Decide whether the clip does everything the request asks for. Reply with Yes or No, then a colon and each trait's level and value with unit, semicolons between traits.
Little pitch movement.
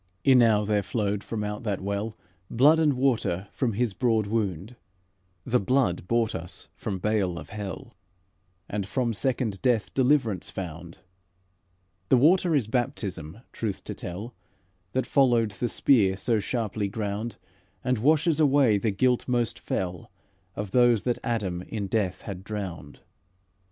No: average, 4.1 semitones